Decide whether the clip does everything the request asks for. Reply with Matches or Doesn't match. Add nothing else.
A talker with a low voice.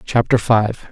Matches